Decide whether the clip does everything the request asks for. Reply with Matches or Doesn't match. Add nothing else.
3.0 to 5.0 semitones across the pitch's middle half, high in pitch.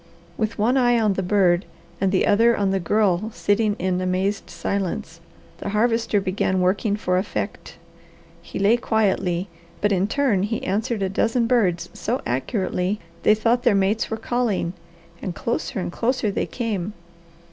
Matches